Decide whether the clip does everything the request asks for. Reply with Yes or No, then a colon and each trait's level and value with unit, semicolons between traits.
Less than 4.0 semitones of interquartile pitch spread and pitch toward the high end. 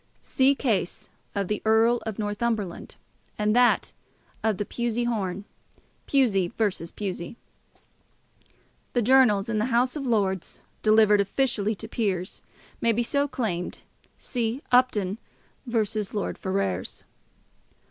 Yes: average, 3.3 semitones; high, 220 Hz